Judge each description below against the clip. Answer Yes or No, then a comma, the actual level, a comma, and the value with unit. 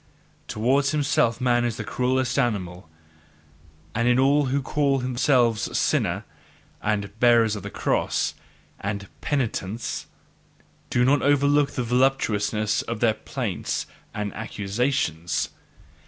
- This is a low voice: Yes, low, 120 Hz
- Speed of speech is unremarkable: No, slow, 115 wpm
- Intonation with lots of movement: No, average, 4.1 semitones